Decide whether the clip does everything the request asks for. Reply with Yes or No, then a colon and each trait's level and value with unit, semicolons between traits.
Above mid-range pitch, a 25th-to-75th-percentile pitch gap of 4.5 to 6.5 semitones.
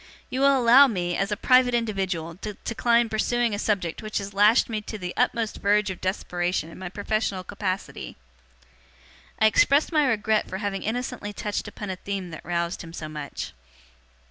No: high, 205 Hz; average, 3.8 semitones